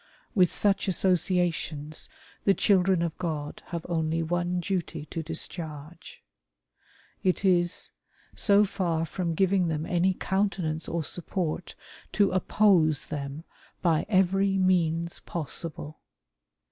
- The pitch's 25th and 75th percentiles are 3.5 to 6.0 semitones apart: No, average, 2.8 semitones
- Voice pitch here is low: No, medium, 175 Hz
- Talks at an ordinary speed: No, slow, 110 wpm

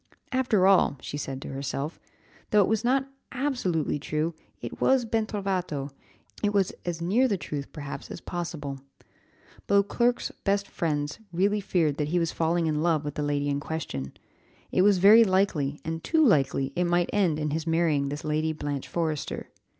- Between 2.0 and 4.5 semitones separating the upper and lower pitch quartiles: No, average, 5.3 semitones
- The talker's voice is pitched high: No, medium, 170 Hz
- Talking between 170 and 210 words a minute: Yes, average, 175 wpm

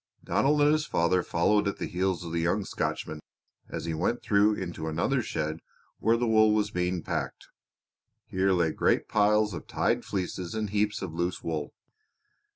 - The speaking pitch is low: Yes, very low, 95 Hz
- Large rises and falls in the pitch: No, average, 3.9 semitones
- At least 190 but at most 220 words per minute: No, average, 175 wpm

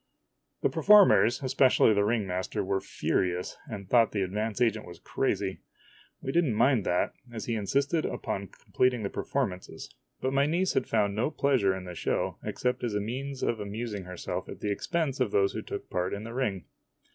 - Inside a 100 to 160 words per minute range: No, average, 190 wpm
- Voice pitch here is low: Yes, low, 110 Hz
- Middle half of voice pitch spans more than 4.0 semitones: Yes, average, 4.8 semitones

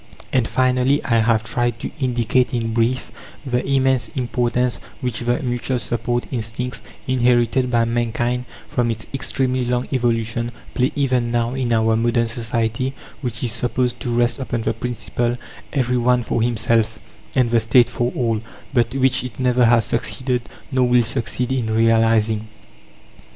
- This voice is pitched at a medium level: No, low, 120 Hz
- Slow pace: No, average, 155 wpm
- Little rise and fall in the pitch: Yes, narrow, 1.5 semitones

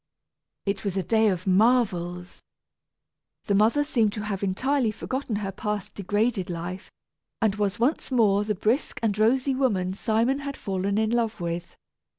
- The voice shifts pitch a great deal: No, average, 3.4 semitones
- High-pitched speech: Yes, high, 210 Hz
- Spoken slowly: No, average, 160 wpm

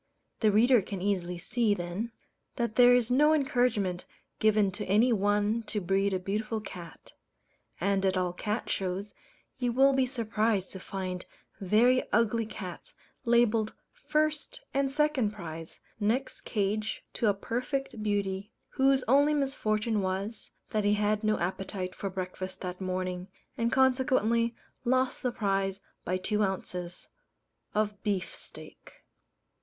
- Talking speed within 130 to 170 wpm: Yes, average, 140 wpm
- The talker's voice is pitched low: No, high, 210 Hz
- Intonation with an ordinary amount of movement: Yes, average, 4.0 semitones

